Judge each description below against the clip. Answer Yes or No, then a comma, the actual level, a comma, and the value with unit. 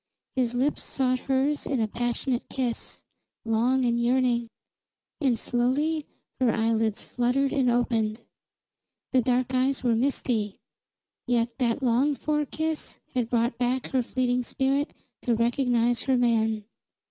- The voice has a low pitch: No, high, 245 Hz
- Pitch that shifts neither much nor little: No, narrow, 2.0 semitones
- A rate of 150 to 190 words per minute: No, slow, 135 wpm